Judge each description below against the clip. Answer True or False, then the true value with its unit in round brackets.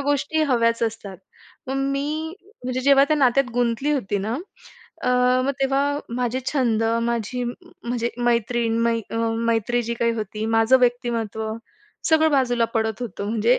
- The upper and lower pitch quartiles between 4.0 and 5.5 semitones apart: False (3.0 semitones)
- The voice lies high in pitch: True (240 Hz)